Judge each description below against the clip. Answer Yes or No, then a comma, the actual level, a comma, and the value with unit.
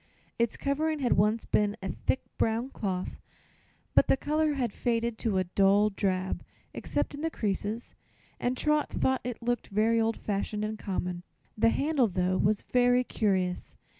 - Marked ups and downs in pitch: No, average, 4.0 semitones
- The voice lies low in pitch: No, high, 225 Hz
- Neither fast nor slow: Yes, average, 165 wpm